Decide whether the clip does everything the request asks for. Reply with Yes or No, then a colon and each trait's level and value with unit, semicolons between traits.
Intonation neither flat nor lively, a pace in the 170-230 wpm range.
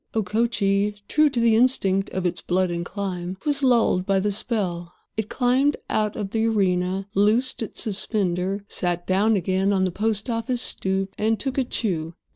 Yes: average, 3.3 semitones; average, 175 wpm